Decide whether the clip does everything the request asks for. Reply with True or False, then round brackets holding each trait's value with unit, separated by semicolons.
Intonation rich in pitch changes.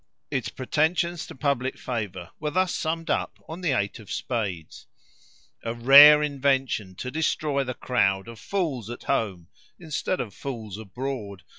True (5.9 semitones)